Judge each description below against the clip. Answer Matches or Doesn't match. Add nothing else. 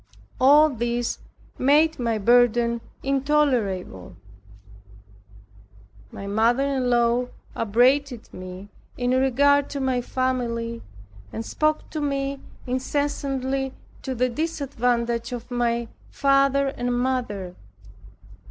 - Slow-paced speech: Matches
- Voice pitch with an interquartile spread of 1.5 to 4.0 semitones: Matches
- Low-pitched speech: Doesn't match